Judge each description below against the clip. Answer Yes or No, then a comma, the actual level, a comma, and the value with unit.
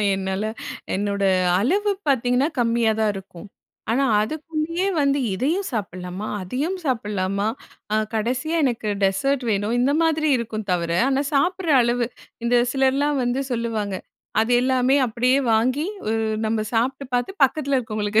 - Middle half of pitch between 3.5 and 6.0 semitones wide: Yes, average, 4.6 semitones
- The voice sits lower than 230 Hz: No, high, 245 Hz